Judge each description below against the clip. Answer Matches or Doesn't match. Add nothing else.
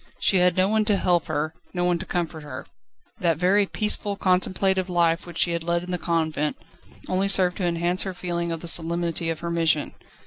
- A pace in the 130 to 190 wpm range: Doesn't match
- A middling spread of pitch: Doesn't match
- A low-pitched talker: Doesn't match